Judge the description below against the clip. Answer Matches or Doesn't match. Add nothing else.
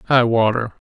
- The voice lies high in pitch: Doesn't match